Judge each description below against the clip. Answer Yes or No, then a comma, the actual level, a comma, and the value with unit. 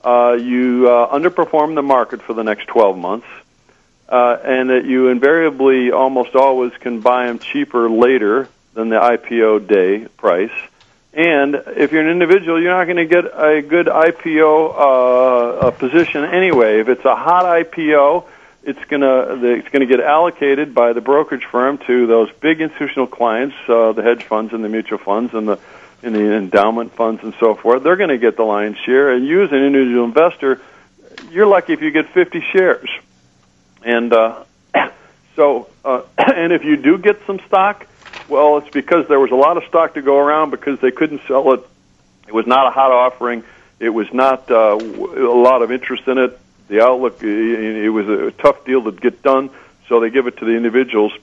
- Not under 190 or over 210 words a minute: Yes, average, 195 wpm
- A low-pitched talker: Yes, low, 130 Hz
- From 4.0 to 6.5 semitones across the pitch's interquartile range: Yes, average, 4.3 semitones